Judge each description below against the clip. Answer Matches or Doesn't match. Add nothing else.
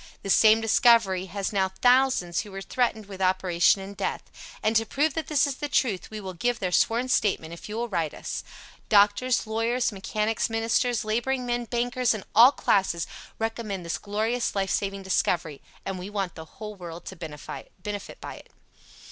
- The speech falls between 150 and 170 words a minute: Doesn't match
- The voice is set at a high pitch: Matches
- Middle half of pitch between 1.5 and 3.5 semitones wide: Doesn't match